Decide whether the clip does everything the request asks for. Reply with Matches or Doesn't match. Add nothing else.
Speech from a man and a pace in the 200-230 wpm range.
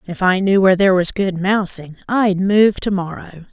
Doesn't match